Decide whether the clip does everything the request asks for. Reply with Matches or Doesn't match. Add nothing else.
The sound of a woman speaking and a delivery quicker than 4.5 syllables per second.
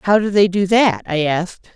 Matches